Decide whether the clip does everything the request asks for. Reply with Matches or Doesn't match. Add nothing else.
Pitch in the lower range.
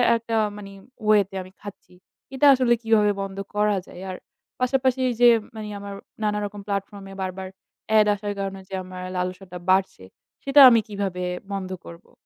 Doesn't match